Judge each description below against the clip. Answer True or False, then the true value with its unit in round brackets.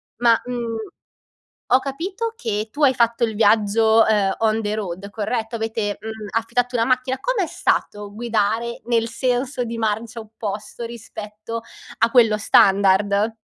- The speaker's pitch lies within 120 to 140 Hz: False (225 Hz)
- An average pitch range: False (2.2 semitones)